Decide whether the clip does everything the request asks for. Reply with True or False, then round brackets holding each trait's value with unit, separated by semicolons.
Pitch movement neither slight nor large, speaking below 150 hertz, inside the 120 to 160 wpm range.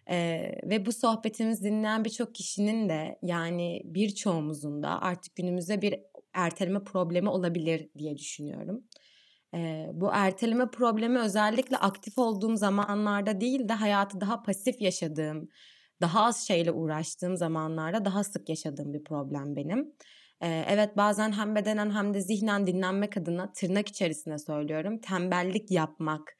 False (4.1 semitones; 195 Hz; 135 wpm)